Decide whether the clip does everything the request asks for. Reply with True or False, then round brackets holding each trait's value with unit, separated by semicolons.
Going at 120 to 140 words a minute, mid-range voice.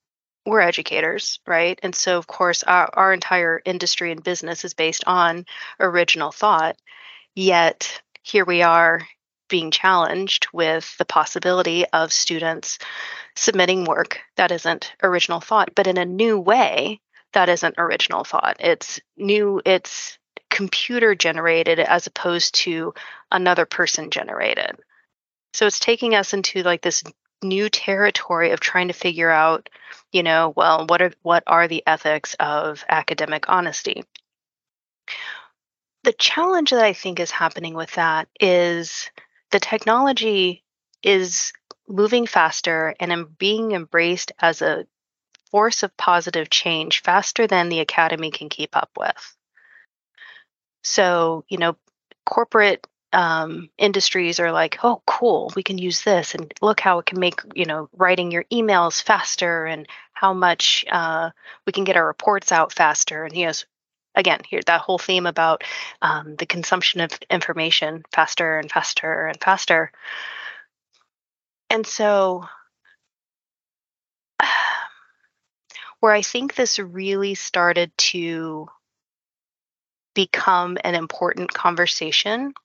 True (135 wpm; 180 Hz)